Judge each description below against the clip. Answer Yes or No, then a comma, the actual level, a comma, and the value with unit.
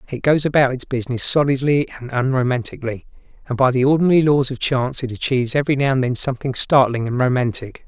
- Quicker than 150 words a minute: Yes, average, 190 wpm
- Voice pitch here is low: Yes, low, 130 Hz